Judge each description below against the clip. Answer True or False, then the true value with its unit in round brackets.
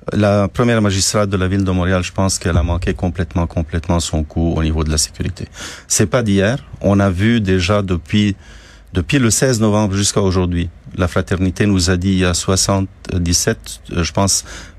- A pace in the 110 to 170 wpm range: False (190 wpm)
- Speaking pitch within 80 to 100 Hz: True (95 Hz)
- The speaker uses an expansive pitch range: False (2.7 semitones)